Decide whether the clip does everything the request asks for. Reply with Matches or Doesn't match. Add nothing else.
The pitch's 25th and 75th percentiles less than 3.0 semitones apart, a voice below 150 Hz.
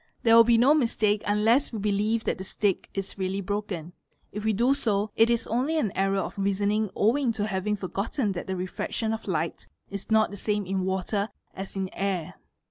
Doesn't match